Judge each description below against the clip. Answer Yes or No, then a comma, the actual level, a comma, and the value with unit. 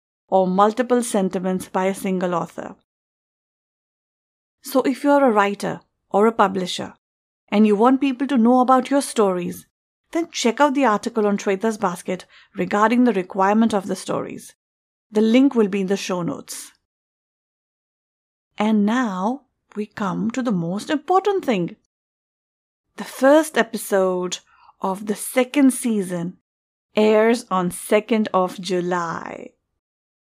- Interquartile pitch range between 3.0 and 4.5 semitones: No, average, 4.9 semitones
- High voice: Yes, high, 210 Hz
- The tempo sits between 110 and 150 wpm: Yes, slow, 135 wpm